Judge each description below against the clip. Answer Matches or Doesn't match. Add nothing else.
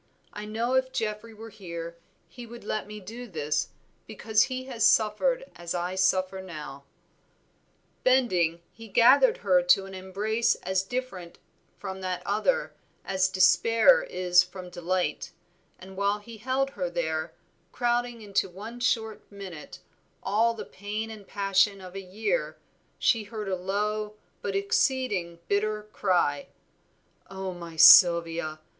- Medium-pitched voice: Doesn't match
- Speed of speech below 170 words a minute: Matches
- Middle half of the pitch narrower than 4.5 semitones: Matches